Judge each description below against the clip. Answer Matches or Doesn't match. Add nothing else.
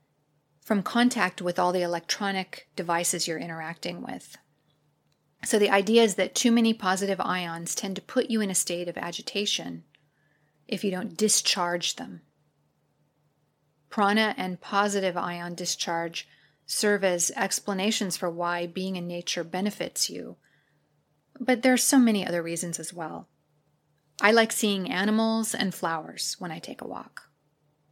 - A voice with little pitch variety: Doesn't match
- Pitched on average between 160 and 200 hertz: Matches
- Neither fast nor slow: Matches